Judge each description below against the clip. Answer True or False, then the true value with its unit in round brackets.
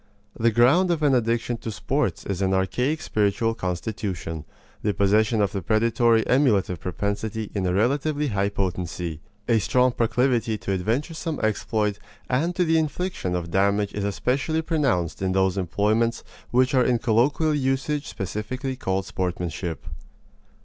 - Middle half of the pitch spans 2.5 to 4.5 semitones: False (5.0 semitones)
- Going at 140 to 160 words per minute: True (145 wpm)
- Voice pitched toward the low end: True (110 Hz)